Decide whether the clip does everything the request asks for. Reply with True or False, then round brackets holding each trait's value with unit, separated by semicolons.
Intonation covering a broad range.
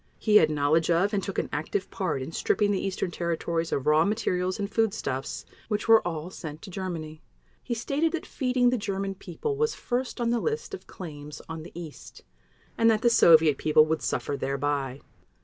True (6.0 semitones)